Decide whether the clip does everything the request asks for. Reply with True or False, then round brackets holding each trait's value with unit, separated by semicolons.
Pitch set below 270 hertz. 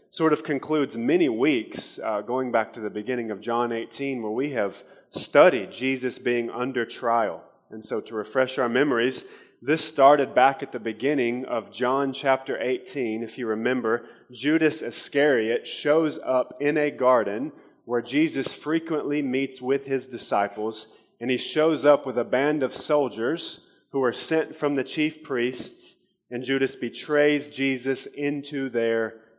True (135 Hz)